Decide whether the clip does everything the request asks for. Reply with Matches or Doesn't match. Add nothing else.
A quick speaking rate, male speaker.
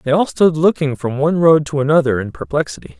Matches